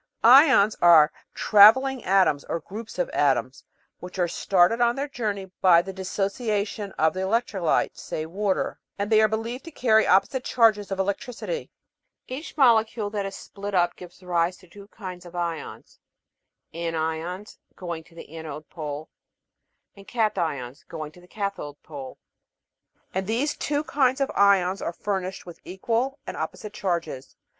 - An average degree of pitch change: Yes, average, 4.4 semitones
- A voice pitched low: No, high, 195 Hz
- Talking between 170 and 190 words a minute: No, average, 155 wpm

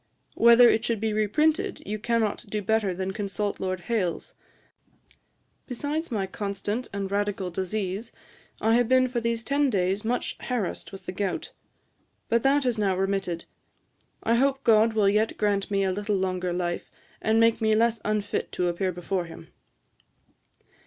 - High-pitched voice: Yes, high, 210 Hz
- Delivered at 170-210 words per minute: No, average, 160 wpm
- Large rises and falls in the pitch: No, average, 3.3 semitones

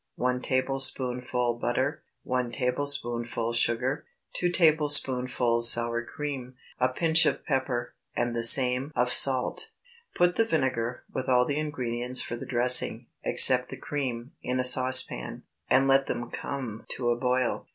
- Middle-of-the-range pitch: No, low, 125 Hz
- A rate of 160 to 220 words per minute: No, average, 140 wpm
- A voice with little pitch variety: Yes, narrow, 2.1 semitones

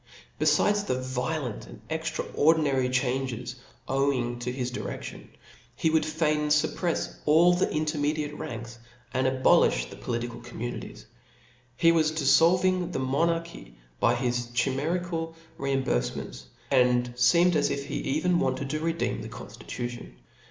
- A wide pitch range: No, average, 4.6 semitones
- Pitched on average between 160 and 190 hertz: No, medium, 140 Hz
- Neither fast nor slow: No, slow, 130 wpm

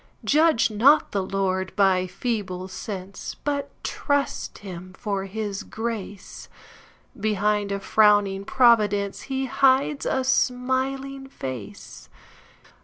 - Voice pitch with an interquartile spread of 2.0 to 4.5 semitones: No, average, 5.2 semitones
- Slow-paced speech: Yes, slow, 90 wpm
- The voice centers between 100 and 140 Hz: No, high, 210 Hz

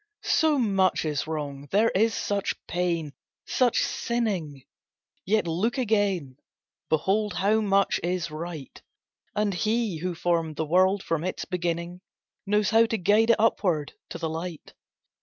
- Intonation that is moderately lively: Yes, average, 4.5 semitones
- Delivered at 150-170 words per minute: No, slow, 135 wpm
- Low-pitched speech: No, medium, 185 Hz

